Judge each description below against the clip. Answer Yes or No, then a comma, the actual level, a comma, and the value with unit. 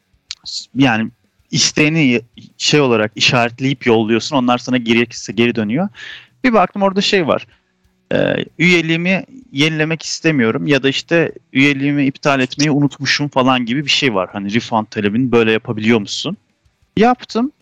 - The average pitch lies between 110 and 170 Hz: Yes, low, 135 Hz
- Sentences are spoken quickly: No, average, 130 wpm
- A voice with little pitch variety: No, average, 4.8 semitones